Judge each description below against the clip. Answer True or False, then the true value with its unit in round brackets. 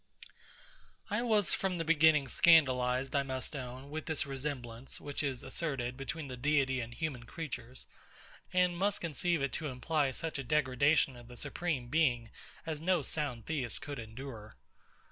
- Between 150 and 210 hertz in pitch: False (140 Hz)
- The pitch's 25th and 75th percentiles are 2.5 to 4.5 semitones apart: True (4.0 semitones)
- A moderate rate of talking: True (160 wpm)